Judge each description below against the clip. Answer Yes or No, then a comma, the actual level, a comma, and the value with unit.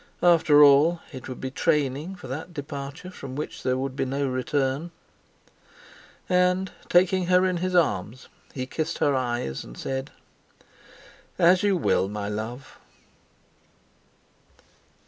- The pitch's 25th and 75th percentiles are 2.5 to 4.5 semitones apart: No, average, 5.2 semitones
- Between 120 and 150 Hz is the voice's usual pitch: Yes, medium, 140 Hz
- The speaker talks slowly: Yes, slow, 130 wpm